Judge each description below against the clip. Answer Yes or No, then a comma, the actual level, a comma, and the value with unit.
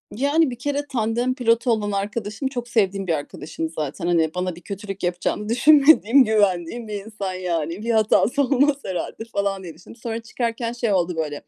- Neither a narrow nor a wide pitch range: Yes, average, 4.8 semitones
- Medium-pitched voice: No, high, 210 Hz